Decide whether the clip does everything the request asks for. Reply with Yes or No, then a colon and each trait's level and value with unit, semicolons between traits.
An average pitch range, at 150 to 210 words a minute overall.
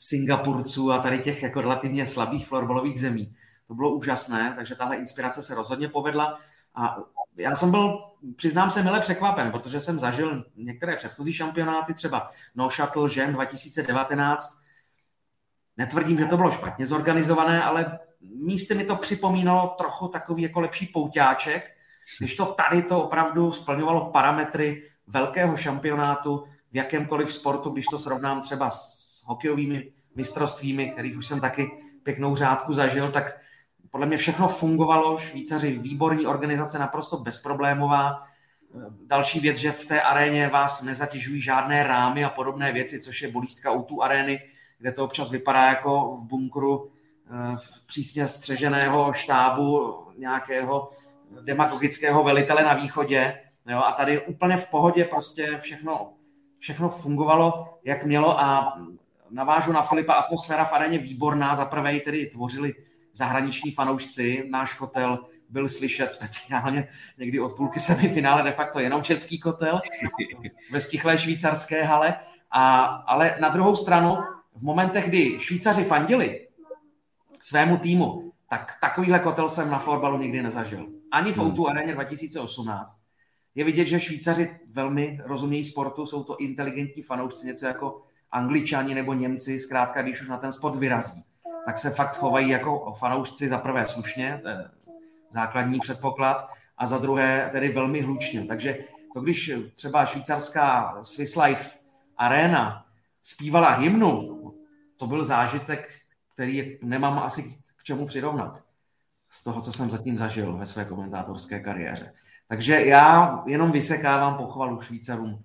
No: average, 3.1 semitones; average, 140 wpm